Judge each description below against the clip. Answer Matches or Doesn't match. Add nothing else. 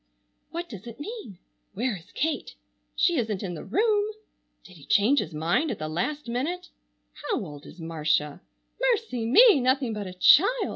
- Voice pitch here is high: Matches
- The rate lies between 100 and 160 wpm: Doesn't match